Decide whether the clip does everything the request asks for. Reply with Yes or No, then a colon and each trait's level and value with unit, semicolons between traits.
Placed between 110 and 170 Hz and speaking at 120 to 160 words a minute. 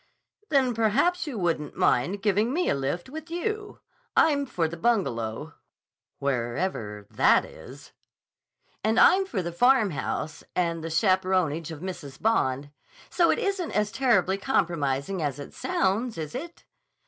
No: high, 190 Hz; average, 140 wpm